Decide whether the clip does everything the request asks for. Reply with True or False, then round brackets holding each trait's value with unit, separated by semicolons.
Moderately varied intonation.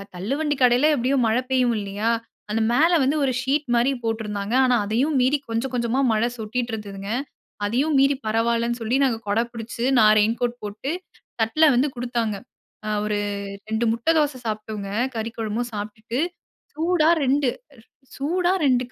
True (3.5 semitones)